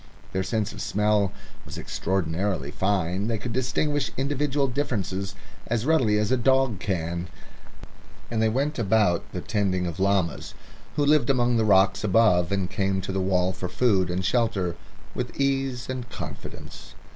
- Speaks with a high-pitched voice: No, low, 105 Hz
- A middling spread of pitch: Yes, average, 4.7 semitones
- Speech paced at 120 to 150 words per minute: No, average, 160 wpm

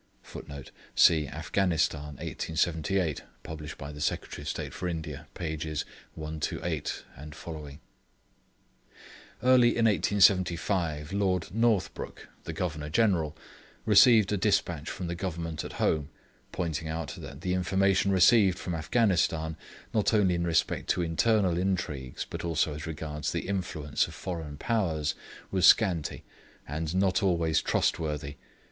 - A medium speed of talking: No, slow, 125 wpm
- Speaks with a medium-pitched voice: No, very low, 85 Hz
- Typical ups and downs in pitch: Yes, average, 3.7 semitones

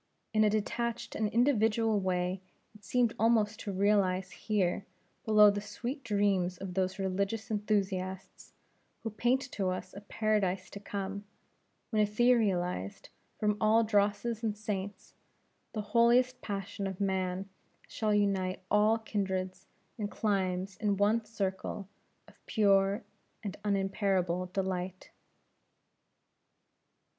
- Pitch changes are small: Yes, narrow, 2.3 semitones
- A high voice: Yes, high, 205 Hz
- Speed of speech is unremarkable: No, slow, 120 wpm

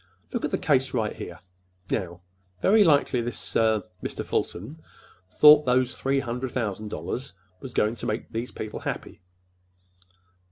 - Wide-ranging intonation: No, average, 3.8 semitones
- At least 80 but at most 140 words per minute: Yes, slow, 135 wpm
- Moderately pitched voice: No, low, 120 Hz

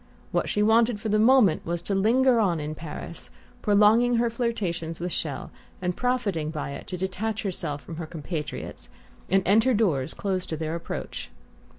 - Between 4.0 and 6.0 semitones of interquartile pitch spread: Yes, average, 5.2 semitones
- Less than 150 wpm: No, average, 175 wpm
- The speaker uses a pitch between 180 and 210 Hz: Yes, high, 190 Hz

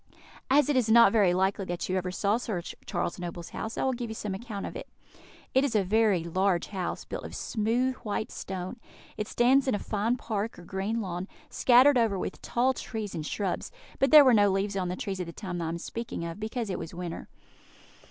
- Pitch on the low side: No, high, 205 Hz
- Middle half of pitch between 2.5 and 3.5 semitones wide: No, average, 4.3 semitones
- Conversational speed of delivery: No, fast, 220 wpm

